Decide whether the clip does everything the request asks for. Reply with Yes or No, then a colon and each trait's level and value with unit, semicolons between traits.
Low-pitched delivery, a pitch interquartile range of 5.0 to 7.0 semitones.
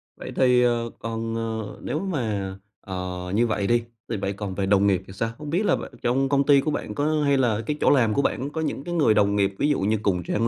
Yes: low, 115 Hz; wide, 5.6 semitones